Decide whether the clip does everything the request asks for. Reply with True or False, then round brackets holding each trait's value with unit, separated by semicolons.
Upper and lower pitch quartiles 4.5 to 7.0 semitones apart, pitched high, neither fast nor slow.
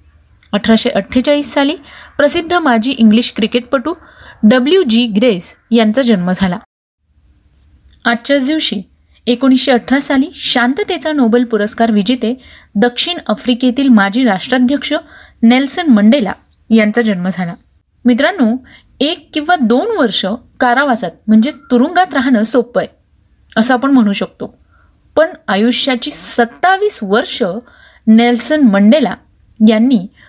False (4.0 semitones; 245 Hz; 105 wpm)